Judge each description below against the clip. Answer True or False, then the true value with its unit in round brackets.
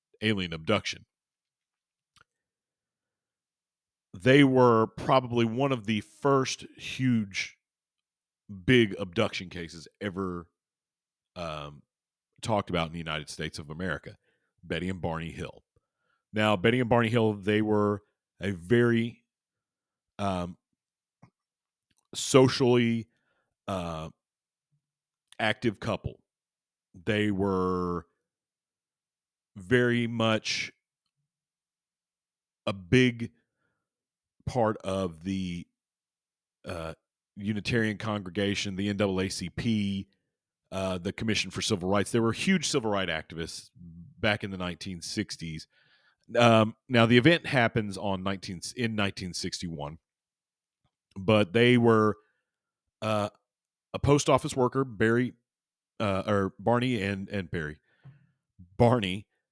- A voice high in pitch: False (105 Hz)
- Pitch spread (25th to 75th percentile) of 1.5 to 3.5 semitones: False (4.1 semitones)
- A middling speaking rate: False (100 wpm)